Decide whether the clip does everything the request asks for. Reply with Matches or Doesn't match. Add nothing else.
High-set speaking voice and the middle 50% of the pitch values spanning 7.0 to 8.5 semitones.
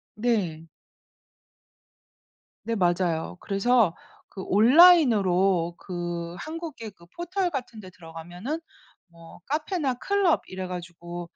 Matches